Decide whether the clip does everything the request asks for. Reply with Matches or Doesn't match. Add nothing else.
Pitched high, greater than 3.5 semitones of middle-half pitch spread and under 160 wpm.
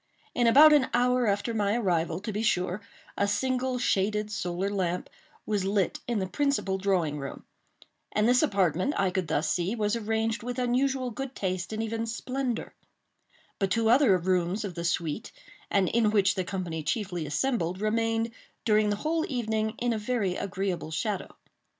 Doesn't match